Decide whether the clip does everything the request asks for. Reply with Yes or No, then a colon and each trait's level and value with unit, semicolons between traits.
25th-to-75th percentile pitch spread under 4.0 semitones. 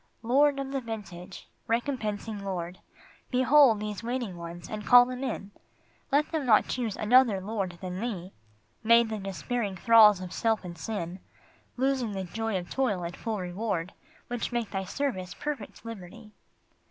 No: average, 4.6 semitones